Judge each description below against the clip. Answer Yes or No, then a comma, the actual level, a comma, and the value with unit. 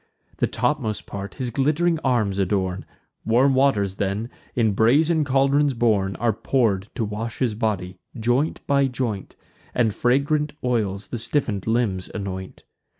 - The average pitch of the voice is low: Yes, low, 115 Hz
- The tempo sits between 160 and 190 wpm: No, average, 140 wpm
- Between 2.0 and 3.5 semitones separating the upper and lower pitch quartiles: No, average, 5.1 semitones